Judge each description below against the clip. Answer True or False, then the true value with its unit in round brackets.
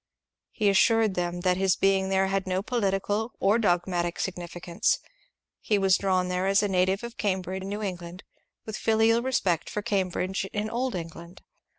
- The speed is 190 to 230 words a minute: False (175 wpm)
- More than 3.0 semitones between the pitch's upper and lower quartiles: False (2.4 semitones)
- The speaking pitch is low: False (190 Hz)